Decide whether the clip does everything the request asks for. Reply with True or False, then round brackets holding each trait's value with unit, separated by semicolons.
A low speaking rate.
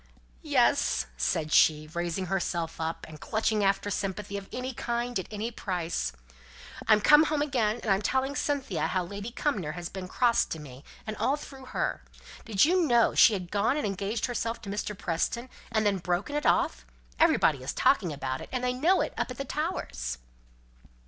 False (190 wpm)